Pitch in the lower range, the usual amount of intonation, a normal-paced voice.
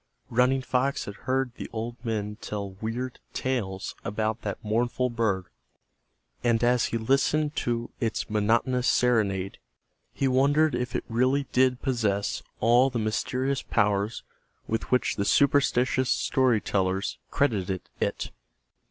No: low, 120 Hz; average, 3.4 semitones; slow, 130 wpm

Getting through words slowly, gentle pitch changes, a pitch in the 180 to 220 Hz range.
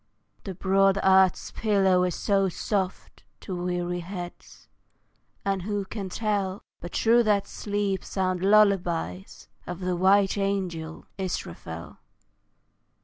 Yes: slow, 115 wpm; narrow, 2.0 semitones; high, 190 Hz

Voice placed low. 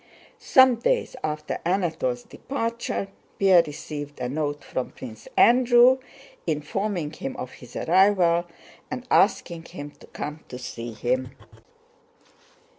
No: medium, 165 Hz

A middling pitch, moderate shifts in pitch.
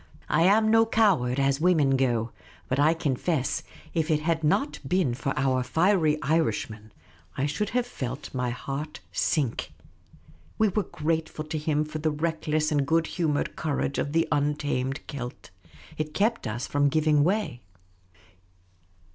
Yes: medium, 150 Hz; average, 3.3 semitones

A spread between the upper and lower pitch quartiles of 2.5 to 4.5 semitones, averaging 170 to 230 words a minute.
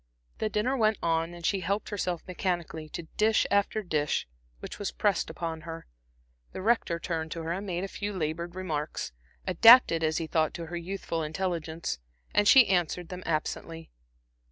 Yes: average, 3.4 semitones; average, 175 wpm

